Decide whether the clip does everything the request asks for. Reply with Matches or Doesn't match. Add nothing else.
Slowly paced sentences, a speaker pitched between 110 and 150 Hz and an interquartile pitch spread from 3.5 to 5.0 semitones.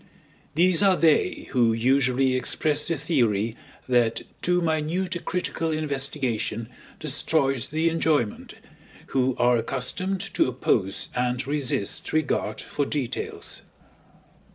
Matches